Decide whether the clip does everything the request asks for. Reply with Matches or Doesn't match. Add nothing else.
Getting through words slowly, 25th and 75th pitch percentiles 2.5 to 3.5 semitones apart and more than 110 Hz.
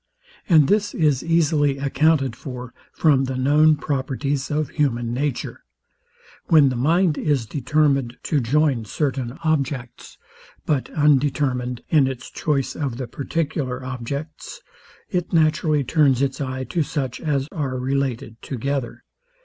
Matches